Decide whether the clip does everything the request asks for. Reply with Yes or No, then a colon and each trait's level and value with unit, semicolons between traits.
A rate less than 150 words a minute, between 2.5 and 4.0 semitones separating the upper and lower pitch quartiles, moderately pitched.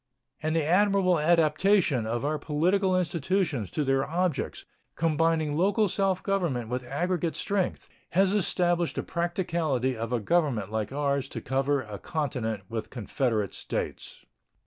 No: average, 140 wpm; wide, 5.5 semitones; medium, 155 Hz